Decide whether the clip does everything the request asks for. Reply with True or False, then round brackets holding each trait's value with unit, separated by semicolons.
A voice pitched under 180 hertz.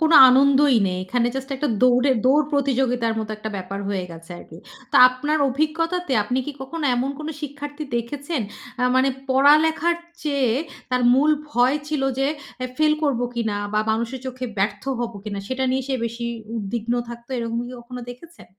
False (260 Hz)